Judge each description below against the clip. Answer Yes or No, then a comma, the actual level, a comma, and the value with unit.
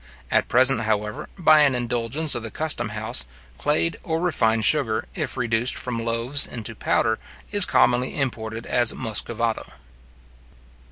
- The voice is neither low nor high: No, low, 120 Hz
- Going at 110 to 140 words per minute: Yes, slow, 135 wpm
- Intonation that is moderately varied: Yes, average, 3.9 semitones